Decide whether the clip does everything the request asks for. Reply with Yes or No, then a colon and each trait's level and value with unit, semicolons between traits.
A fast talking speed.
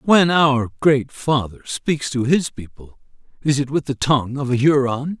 No: average, 185 wpm